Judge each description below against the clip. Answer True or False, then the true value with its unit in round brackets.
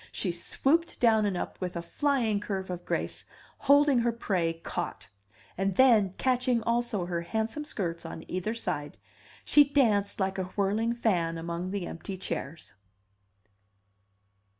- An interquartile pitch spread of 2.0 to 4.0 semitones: False (5.1 semitones)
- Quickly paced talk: False (145 wpm)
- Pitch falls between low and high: False (200 Hz)